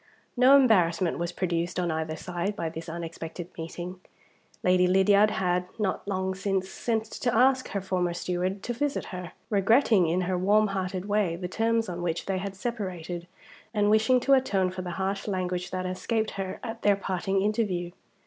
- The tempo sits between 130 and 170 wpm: No, average, 180 wpm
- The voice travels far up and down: No, average, 3.0 semitones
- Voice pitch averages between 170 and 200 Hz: Yes, high, 190 Hz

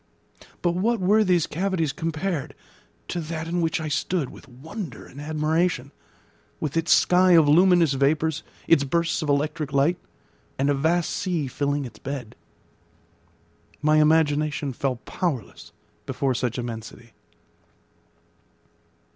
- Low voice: No, medium, 155 Hz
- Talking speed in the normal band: No, slow, 130 wpm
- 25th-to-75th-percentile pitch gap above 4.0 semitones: No, average, 3.6 semitones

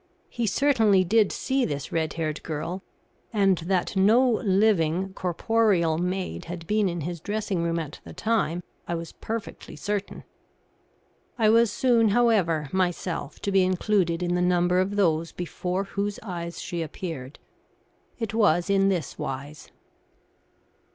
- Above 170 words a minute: No, average, 145 wpm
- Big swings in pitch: No, average, 3.7 semitones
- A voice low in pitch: No, medium, 185 Hz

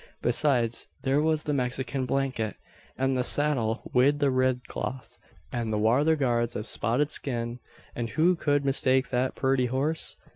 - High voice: No, low, 130 Hz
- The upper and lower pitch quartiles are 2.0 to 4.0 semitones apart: Yes, average, 2.9 semitones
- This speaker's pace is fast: No, average, 155 wpm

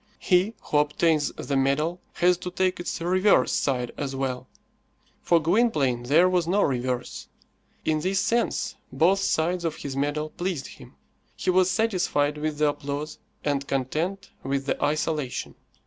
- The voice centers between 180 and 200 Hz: No, medium, 155 Hz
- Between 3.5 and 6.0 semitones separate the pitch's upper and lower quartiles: Yes, average, 4.4 semitones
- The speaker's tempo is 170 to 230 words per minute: No, average, 150 wpm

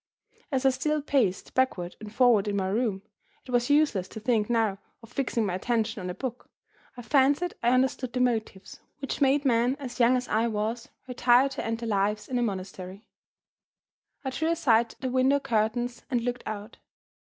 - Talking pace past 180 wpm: Yes, average, 190 wpm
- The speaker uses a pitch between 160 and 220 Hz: No, high, 240 Hz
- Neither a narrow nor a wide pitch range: Yes, average, 3.3 semitones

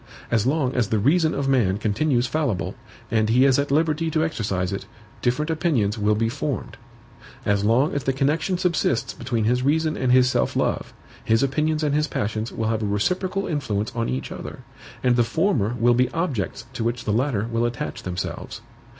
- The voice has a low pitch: Yes, low, 125 Hz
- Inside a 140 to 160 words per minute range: No, average, 195 wpm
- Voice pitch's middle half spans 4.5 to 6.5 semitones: Yes, wide, 5.5 semitones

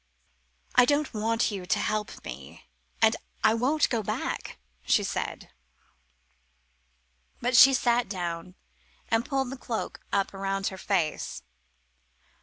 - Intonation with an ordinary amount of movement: Yes, average, 4.1 semitones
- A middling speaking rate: No, slow, 125 wpm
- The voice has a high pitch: Yes, high, 220 Hz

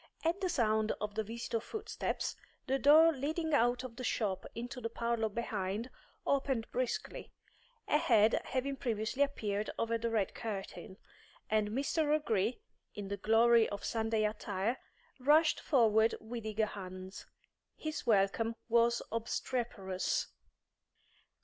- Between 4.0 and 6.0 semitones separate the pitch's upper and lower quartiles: No, average, 3.5 semitones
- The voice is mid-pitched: No, high, 230 Hz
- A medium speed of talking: No, slow, 130 wpm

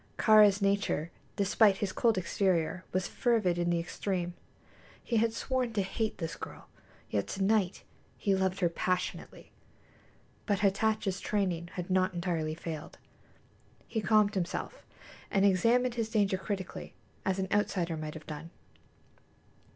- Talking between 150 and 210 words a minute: No, average, 140 wpm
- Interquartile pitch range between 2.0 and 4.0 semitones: Yes, average, 3.3 semitones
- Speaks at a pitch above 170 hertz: Yes, high, 190 Hz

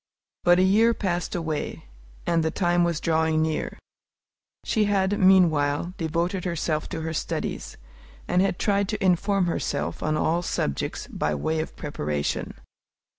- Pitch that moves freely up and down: No, average, 3.0 semitones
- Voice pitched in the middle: Yes, medium, 170 Hz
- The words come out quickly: No, average, 145 wpm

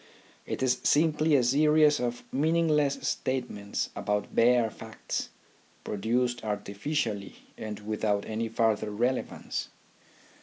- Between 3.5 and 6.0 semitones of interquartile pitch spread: Yes, average, 5.1 semitones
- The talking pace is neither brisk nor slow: No, slow, 105 wpm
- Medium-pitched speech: No, low, 120 Hz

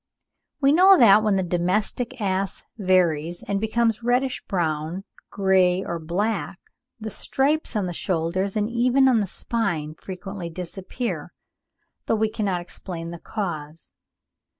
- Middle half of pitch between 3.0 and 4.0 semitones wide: No, average, 4.5 semitones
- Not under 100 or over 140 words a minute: Yes, slow, 135 wpm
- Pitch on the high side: Yes, high, 195 Hz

